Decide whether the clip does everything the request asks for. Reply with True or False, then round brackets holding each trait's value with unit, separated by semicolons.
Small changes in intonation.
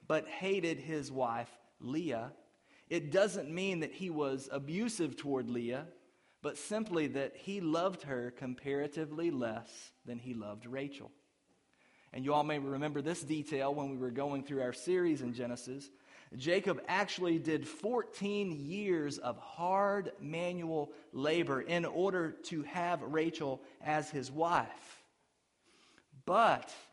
False (4.1 semitones)